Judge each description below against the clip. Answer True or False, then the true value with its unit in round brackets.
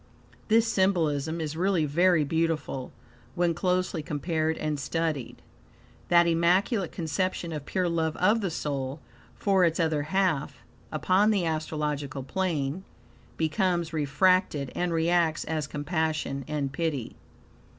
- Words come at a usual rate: False (120 wpm)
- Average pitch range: True (3.3 semitones)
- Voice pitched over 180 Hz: False (160 Hz)